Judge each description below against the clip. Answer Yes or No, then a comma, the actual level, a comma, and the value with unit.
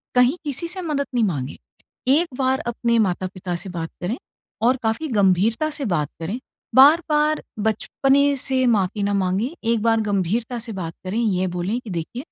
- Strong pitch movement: Yes, wide, 6.0 semitones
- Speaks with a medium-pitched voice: No, high, 225 Hz